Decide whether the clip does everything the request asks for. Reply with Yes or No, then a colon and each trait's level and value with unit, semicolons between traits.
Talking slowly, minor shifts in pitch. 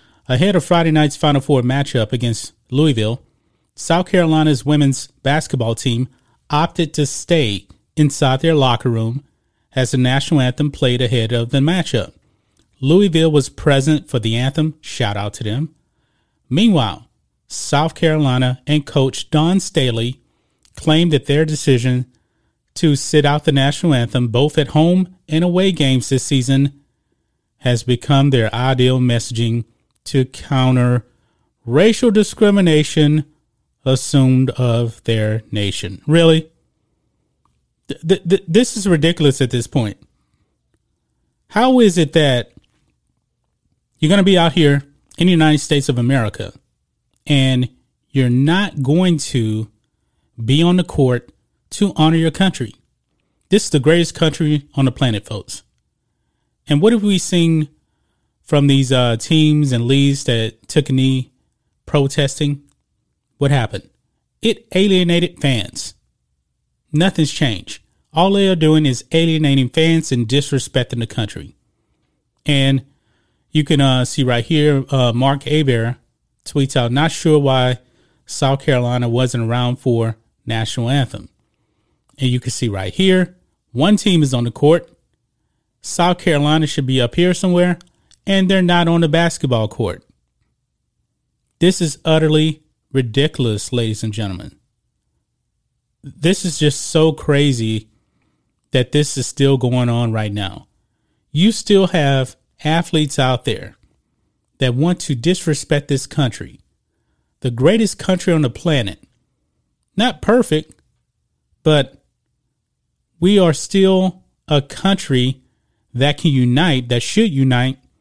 No: slow, 130 wpm; average, 4.5 semitones